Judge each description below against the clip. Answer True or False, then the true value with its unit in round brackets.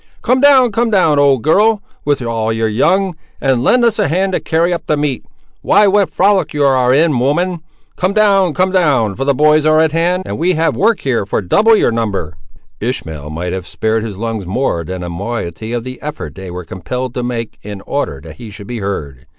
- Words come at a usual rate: False (215 wpm)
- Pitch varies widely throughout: True (8.6 semitones)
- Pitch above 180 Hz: False (135 Hz)